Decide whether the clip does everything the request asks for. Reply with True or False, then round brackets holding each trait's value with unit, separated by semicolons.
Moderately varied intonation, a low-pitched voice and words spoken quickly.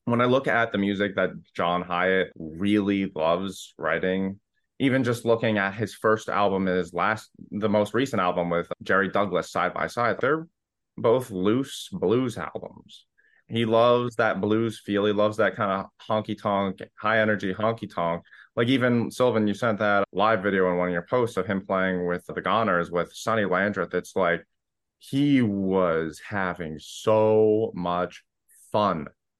False (3.5 semitones; 105 Hz; 165 wpm)